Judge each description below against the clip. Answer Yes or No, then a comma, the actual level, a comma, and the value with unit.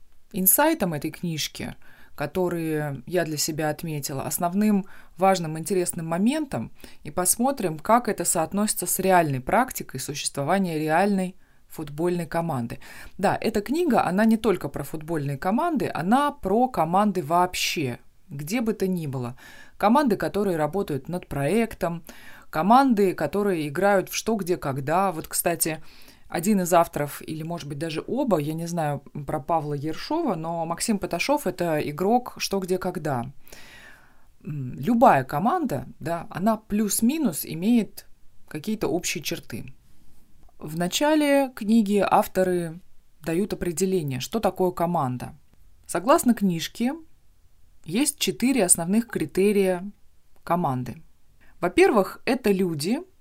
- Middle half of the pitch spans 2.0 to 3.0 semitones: No, average, 4.6 semitones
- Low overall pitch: No, medium, 180 Hz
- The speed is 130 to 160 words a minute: No, average, 120 wpm